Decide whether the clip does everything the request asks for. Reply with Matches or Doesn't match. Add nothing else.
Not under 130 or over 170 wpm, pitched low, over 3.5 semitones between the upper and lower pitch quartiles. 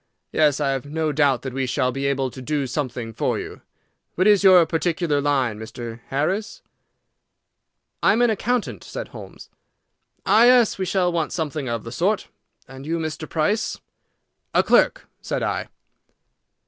Doesn't match